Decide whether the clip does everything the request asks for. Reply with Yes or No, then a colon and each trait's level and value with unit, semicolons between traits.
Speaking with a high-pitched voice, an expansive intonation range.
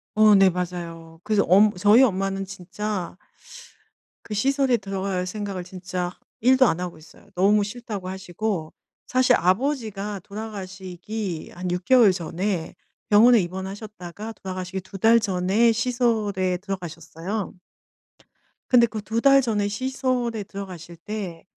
No: high, 195 Hz; average, 3.3 semitones